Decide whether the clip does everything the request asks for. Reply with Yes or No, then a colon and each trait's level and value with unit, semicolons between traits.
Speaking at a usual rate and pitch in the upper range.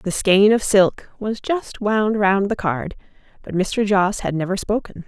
Yes: average, 190 wpm; high, 200 Hz